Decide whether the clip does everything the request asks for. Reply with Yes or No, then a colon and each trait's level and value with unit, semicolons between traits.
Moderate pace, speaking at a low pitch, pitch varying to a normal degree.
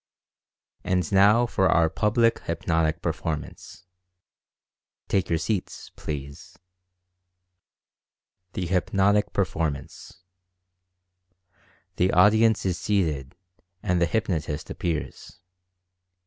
No: slow, 80 wpm; very low, 90 Hz; average, 3.9 semitones